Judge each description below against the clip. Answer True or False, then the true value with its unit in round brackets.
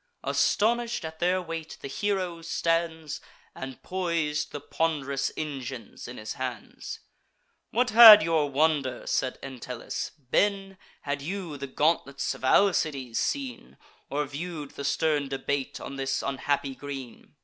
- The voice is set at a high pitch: False (150 Hz)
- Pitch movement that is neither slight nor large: True (4.1 semitones)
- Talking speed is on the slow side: True (130 wpm)